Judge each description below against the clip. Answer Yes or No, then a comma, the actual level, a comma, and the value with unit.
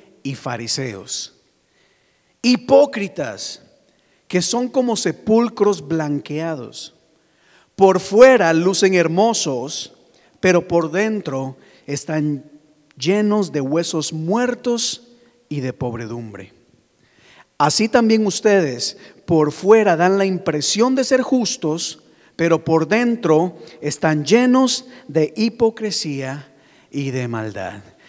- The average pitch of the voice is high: No, medium, 165 Hz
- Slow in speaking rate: Yes, slow, 95 wpm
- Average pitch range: No, wide, 6.7 semitones